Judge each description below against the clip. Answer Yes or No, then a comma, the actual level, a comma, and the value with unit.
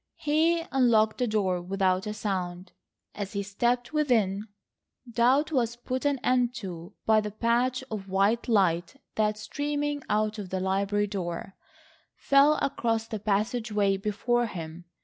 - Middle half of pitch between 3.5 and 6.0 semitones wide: Yes, average, 4.0 semitones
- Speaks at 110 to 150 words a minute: Yes, average, 145 wpm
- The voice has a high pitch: Yes, high, 215 Hz